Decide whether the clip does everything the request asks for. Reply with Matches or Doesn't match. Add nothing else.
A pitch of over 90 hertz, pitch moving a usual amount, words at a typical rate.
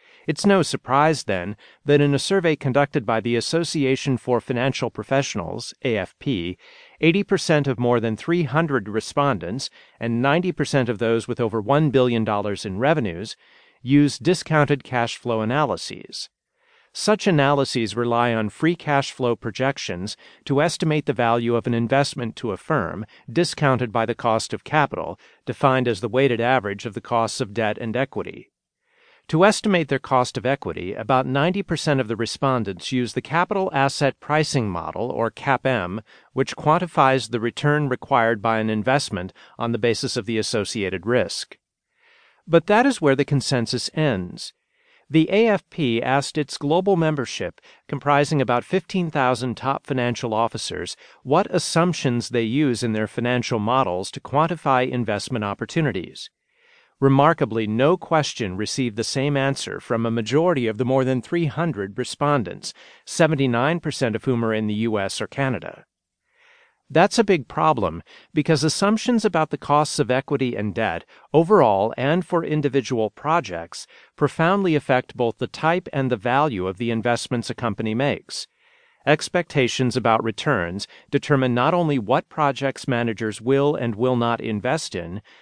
Matches